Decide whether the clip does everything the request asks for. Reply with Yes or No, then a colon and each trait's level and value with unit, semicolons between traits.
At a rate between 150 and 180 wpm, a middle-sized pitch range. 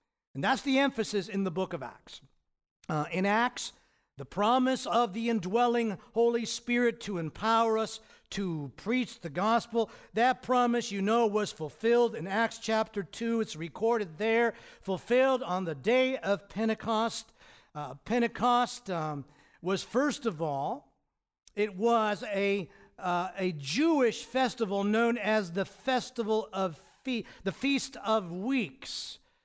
No: average, 140 wpm; average, 3.6 semitones